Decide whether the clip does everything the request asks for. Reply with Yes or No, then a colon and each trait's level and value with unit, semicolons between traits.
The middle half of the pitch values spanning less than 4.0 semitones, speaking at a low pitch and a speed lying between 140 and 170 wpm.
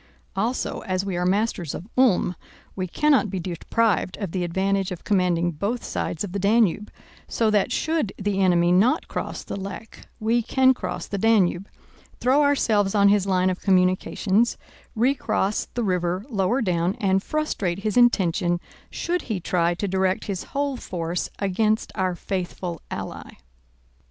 No: average, 3.6 semitones; high, 195 Hz; average, 155 wpm